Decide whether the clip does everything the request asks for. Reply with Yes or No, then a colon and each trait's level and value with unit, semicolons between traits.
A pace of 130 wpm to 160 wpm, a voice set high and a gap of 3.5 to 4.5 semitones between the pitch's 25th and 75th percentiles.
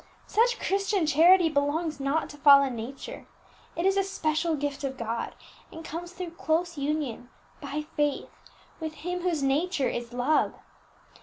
Yes: average, 150 wpm; very high, 310 Hz; average, 3.8 semitones